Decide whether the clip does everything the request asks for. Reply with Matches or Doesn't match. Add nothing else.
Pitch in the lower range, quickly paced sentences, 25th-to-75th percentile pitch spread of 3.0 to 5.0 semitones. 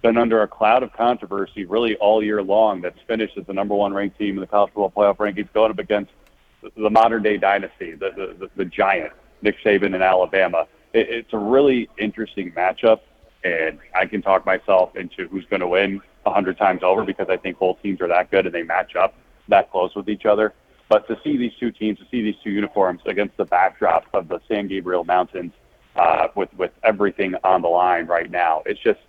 Doesn't match